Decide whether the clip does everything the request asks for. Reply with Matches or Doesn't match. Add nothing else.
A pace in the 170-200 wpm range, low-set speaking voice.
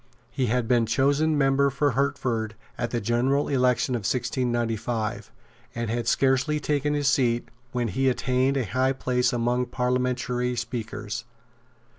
Doesn't match